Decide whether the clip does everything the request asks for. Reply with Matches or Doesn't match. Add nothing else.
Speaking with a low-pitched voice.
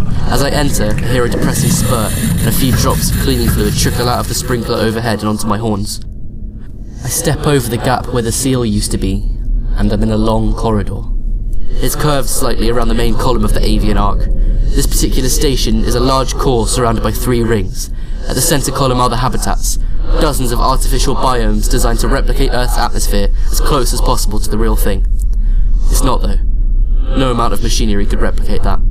Matches